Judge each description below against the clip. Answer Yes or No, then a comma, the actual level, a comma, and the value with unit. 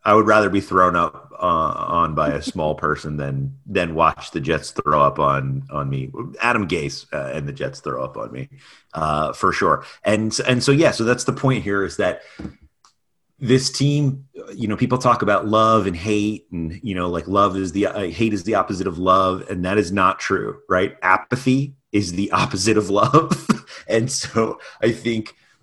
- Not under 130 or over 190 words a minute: No, average, 200 wpm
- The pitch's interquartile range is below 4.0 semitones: No, average, 4.6 semitones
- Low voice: Yes, low, 105 Hz